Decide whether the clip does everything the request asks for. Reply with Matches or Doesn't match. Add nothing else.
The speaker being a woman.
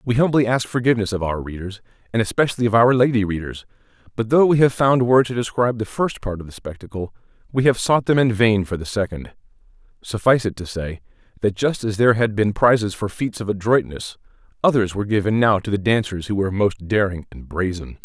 Doesn't match